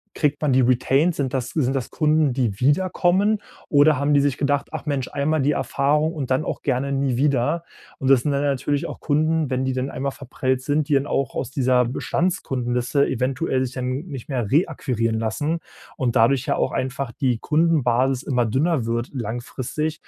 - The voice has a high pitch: No, low, 135 Hz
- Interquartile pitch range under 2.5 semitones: No, average, 2.8 semitones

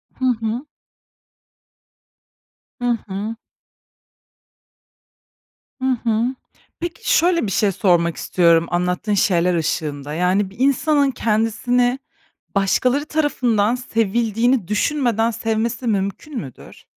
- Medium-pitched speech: No, high, 225 Hz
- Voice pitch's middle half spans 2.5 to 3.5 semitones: No, average, 4.6 semitones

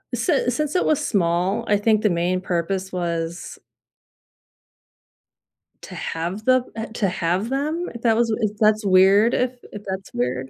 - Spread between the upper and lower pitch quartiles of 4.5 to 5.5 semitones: Yes, average, 4.8 semitones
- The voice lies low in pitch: No, high, 200 Hz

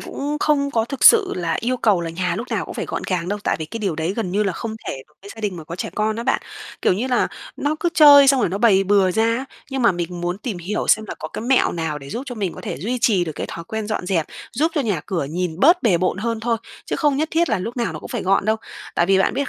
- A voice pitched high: Yes, high, 210 Hz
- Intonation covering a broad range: Yes, wide, 5.7 semitones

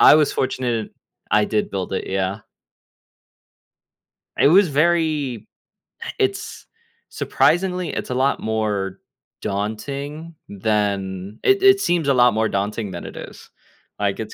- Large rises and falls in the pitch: Yes, wide, 7.6 semitones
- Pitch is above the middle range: No, low, 115 Hz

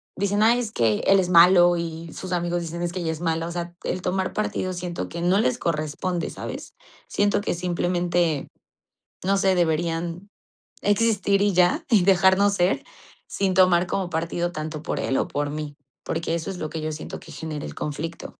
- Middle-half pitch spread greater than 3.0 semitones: No, narrow, 2.5 semitones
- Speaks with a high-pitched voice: No, medium, 175 Hz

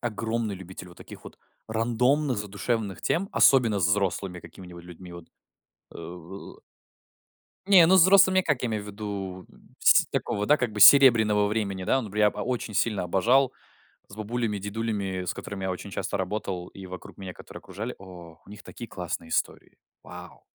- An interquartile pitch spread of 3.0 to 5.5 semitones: Yes, average, 3.9 semitones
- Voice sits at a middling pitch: No, low, 105 Hz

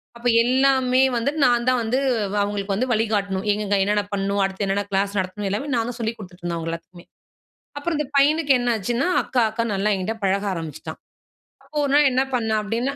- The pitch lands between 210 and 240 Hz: Yes, high, 215 Hz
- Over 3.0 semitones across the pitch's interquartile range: Yes, average, 4.1 semitones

